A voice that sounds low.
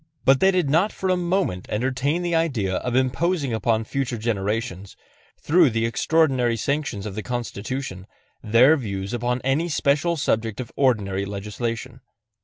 Yes: low, 125 Hz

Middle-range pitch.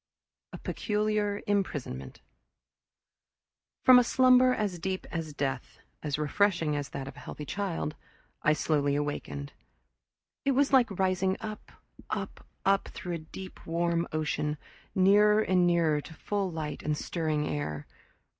Yes: medium, 170 Hz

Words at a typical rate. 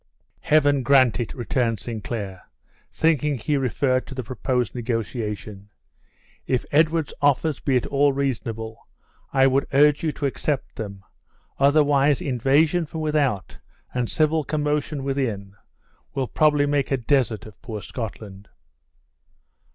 No: slow, 130 wpm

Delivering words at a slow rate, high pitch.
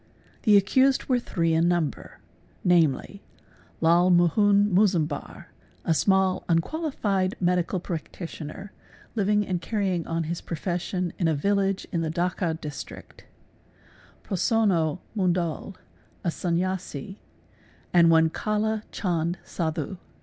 No: slow, 110 wpm; medium, 180 Hz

